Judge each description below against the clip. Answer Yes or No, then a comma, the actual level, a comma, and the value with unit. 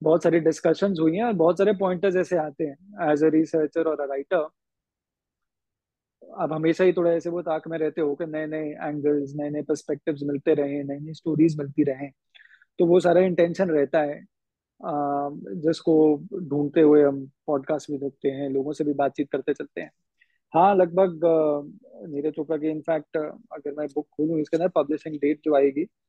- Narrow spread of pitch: Yes, narrow, 2.3 semitones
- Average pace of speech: Yes, average, 175 wpm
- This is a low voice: No, medium, 155 Hz